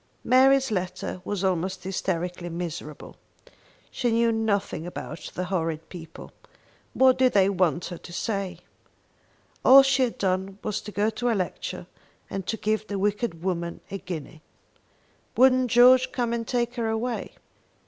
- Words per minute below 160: Yes, average, 150 wpm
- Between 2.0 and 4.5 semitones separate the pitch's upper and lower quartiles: No, average, 4.9 semitones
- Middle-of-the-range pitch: No, high, 200 Hz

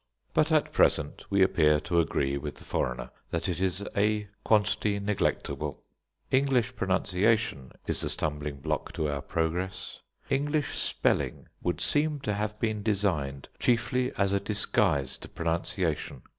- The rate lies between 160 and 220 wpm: No, average, 145 wpm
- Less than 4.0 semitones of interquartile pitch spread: No, wide, 5.5 semitones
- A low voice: Yes, very low, 95 Hz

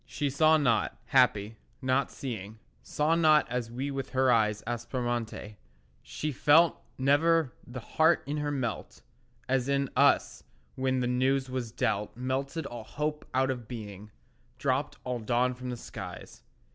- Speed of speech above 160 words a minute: No, average, 145 wpm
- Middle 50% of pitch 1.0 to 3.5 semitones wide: Yes, average, 2.9 semitones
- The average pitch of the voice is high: No, low, 130 Hz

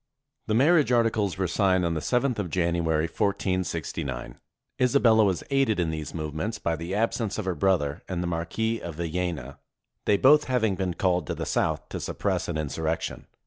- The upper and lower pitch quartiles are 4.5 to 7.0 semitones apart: Yes, average, 5.1 semitones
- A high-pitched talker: No, very low, 95 Hz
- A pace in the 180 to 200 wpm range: Yes, average, 185 wpm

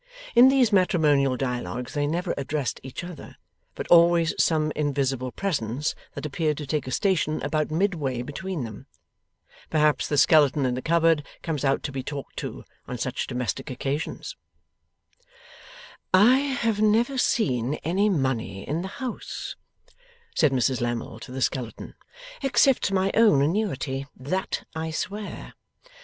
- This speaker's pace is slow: No, average, 145 wpm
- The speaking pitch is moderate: Yes, medium, 150 Hz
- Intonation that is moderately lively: No, wide, 5.9 semitones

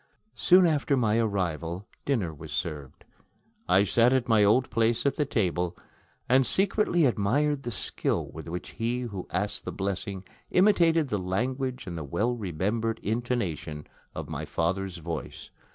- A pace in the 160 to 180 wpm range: No, average, 150 wpm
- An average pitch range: No, wide, 6.1 semitones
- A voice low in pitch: Yes, low, 110 Hz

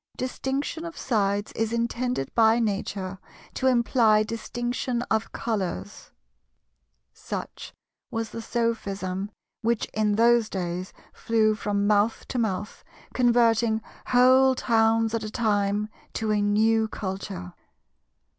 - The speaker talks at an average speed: No, slow, 110 wpm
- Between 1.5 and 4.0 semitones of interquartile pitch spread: Yes, average, 2.7 semitones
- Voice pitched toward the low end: No, high, 220 Hz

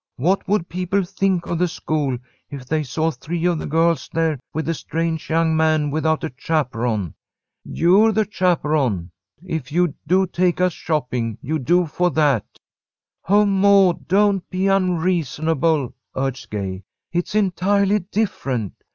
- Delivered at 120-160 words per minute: Yes, average, 150 wpm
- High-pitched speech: No, medium, 165 Hz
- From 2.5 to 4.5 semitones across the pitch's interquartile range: Yes, average, 3.9 semitones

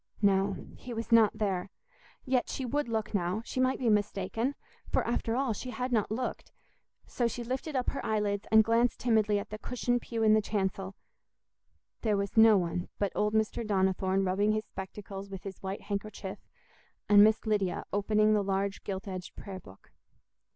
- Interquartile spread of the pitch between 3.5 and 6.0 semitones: No, average, 2.8 semitones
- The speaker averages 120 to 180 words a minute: Yes, average, 170 wpm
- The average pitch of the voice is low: No, high, 210 Hz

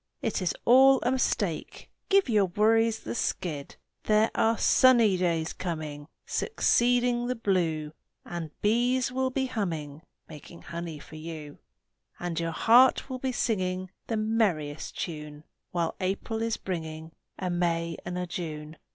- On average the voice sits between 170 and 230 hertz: Yes, medium, 185 Hz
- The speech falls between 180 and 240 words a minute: No, average, 145 wpm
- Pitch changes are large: Yes, wide, 6.1 semitones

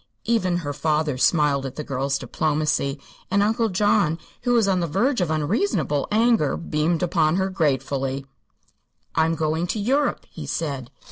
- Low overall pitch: No, medium, 160 Hz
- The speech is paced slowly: No, average, 155 wpm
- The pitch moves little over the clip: No, wide, 5.4 semitones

